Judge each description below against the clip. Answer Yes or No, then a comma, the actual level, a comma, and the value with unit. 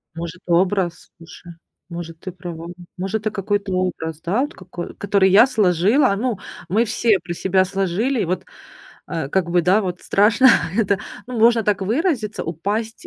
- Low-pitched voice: No, high, 190 Hz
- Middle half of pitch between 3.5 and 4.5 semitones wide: Yes, average, 3.8 semitones